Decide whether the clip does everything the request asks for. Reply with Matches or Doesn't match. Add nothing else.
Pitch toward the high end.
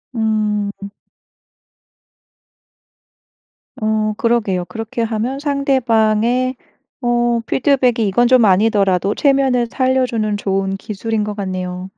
Matches